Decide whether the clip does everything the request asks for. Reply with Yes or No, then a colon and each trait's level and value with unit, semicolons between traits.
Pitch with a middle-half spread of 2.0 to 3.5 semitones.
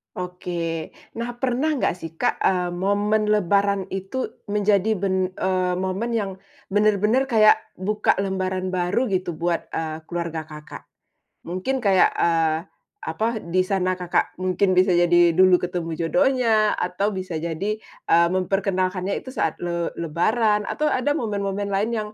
Yes: average, 3.2 semitones